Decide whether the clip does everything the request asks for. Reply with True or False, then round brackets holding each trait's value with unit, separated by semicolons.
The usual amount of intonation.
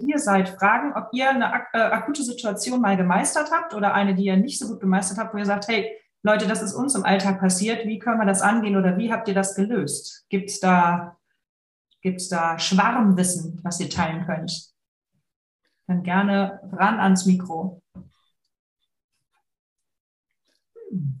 True (3.1 semitones)